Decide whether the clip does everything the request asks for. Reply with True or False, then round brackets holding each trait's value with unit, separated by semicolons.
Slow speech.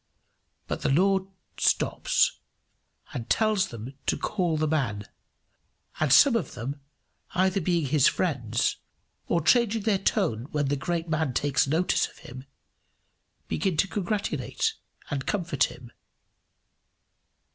True (125 wpm)